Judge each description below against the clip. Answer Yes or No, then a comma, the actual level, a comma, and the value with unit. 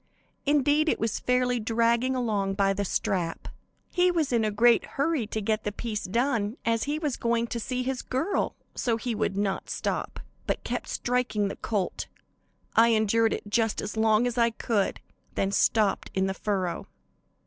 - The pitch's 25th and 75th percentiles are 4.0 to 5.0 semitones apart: No, average, 3.3 semitones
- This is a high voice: Yes, high, 230 Hz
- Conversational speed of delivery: Yes, average, 175 wpm